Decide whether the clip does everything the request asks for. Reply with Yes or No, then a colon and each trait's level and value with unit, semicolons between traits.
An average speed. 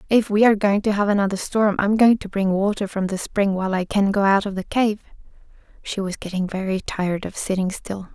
No: fast, 245 wpm